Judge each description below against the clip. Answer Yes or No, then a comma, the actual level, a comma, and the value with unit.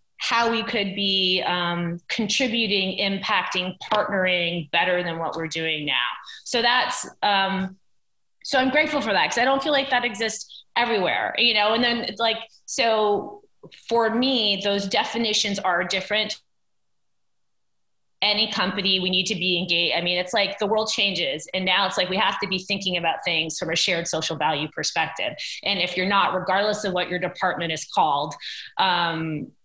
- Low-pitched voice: No, high, 195 Hz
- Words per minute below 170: No, average, 175 wpm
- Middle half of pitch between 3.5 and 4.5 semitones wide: Yes, average, 4.0 semitones